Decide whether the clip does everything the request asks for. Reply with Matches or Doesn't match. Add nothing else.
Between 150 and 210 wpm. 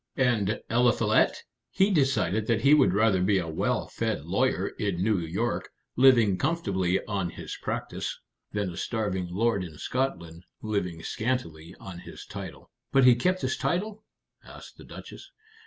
Matches